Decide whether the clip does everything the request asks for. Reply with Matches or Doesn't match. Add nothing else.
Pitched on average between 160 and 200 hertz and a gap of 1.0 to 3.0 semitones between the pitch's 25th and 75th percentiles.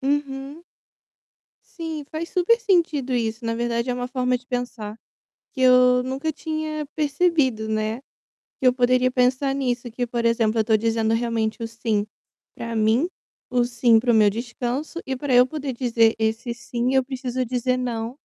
Doesn't match